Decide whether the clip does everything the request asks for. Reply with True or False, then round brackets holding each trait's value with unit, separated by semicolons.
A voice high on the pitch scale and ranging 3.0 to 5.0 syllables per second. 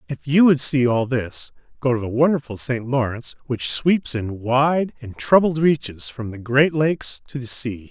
False (130 Hz; 4.6 syllables/s)